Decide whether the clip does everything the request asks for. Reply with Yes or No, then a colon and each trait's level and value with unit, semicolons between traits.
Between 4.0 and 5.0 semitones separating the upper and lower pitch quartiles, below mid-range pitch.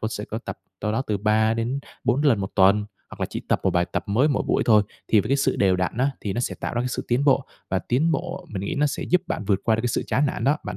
Yes: average, 4.7 semitones; low, 115 Hz